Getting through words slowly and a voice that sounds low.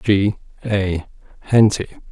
Yes: slow, 85 wpm; low, 100 Hz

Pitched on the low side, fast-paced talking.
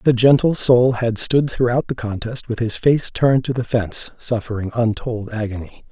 No: low, 120 Hz; average, 185 wpm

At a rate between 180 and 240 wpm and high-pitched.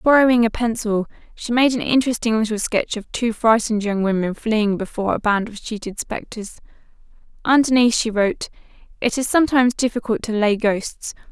No: average, 165 wpm; high, 225 Hz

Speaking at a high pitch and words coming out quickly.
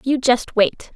No: very high, 250 Hz; average, 190 wpm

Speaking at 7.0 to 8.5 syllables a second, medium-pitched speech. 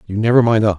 No: 7.5 syllables/s; low, 110 Hz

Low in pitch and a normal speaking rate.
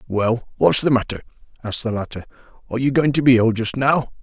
No: low, 120 Hz; fast, 215 wpm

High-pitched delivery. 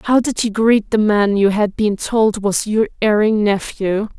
Yes: high, 210 Hz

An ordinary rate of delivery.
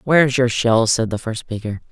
No: fast, 220 wpm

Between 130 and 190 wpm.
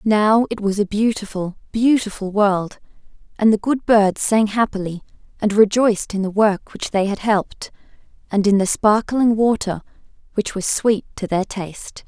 Yes: average, 165 wpm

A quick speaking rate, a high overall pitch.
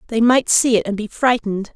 Yes: fast, 240 wpm; high, 230 Hz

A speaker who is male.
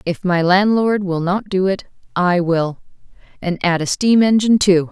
No: female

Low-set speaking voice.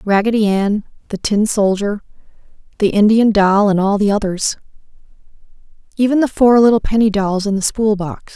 No: high, 210 Hz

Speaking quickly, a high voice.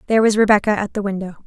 Yes: fast, 245 wpm; high, 205 Hz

